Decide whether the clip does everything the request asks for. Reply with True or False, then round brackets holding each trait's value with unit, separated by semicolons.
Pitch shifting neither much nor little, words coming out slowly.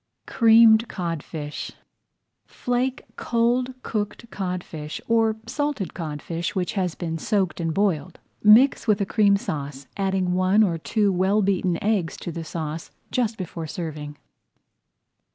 True (4.8 semitones; 130 wpm)